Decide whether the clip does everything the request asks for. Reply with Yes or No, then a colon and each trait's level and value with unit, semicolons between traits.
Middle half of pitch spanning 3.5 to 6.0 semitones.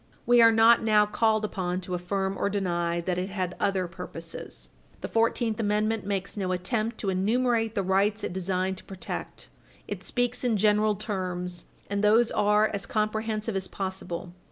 No: average, 2.8 semitones